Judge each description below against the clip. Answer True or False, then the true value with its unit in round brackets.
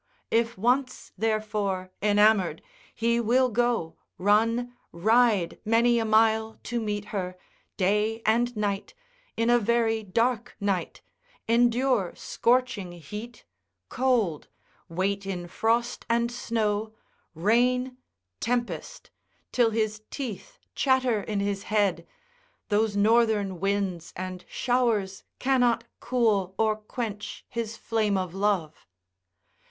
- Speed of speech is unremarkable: False (110 wpm)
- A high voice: True (220 Hz)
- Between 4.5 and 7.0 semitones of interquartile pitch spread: False (3.0 semitones)